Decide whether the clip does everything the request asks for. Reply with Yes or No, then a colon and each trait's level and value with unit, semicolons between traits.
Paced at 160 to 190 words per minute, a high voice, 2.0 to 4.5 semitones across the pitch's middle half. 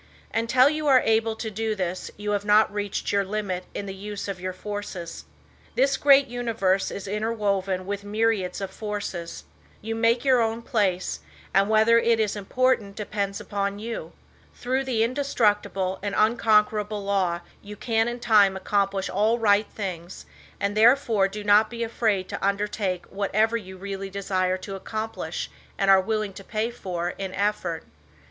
Yes: average, 165 wpm; high, 205 Hz; narrow, 2.5 semitones